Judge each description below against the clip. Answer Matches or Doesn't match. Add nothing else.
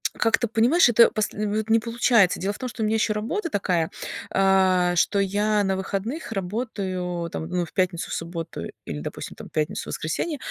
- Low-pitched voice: Doesn't match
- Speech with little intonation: Doesn't match